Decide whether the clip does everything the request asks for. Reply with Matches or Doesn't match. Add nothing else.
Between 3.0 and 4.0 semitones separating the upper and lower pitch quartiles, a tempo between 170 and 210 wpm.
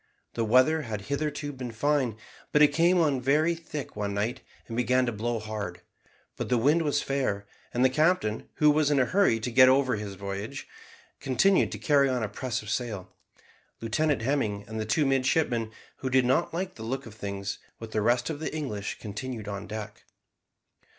Doesn't match